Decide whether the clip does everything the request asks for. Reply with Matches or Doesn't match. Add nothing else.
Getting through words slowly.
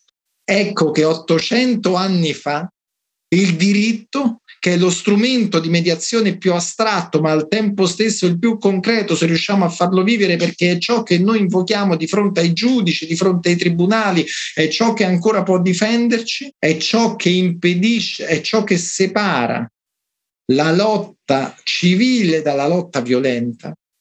Doesn't match